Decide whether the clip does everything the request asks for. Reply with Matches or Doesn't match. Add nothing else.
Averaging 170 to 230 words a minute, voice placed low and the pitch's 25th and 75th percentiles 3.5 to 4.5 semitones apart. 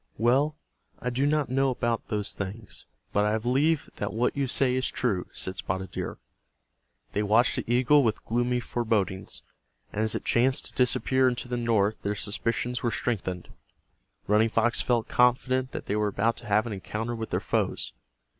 Doesn't match